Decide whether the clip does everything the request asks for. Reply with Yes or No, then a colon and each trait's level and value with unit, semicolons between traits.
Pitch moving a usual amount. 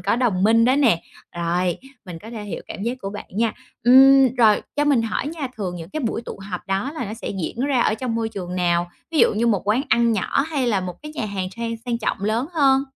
Yes: average, 4.8 semitones